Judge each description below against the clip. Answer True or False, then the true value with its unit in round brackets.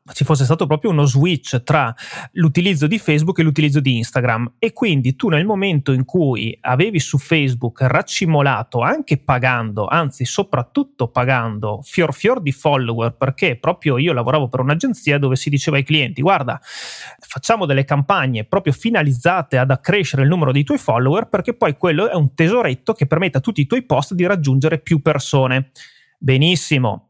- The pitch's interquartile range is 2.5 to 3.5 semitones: False (4.3 semitones)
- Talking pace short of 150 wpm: False (170 wpm)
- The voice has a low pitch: False (145 Hz)